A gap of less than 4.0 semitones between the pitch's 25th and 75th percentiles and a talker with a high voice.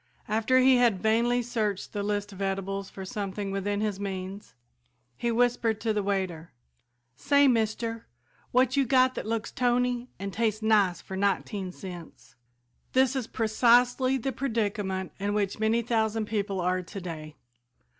Yes: average, 3.5 semitones; high, 215 Hz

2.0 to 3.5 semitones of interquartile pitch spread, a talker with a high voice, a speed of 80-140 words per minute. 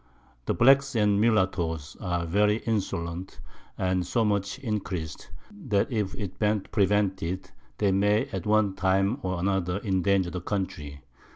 No: narrow, 2.5 semitones; low, 100 Hz; slow, 135 wpm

